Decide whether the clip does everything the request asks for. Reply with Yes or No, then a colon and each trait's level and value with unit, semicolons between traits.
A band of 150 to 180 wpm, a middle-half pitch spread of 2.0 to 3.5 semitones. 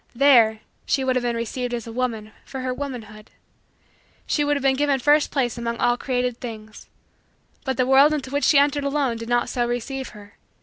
No: fast, 205 wpm; average, 2.9 semitones